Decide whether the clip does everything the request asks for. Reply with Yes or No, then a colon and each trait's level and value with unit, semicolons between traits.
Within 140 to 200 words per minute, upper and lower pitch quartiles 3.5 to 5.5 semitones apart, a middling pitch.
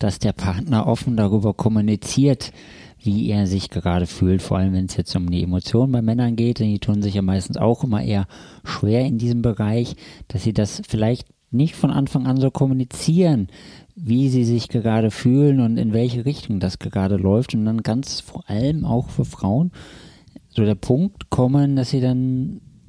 No: fast, 190 wpm; average, 4.1 semitones; low, 115 Hz